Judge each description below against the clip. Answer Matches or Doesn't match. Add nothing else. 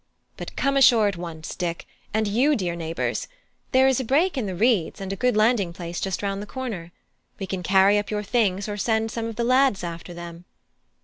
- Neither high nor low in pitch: Doesn't match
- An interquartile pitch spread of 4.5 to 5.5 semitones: Matches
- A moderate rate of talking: Doesn't match